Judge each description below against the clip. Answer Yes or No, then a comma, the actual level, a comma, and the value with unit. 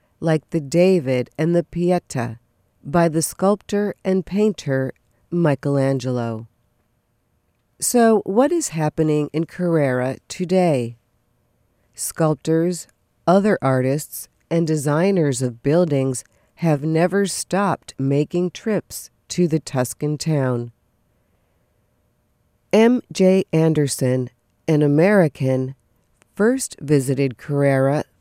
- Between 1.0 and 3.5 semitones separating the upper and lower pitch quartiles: No, wide, 5.5 semitones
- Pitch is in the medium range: Yes, medium, 150 Hz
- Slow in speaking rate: Yes, slow, 90 wpm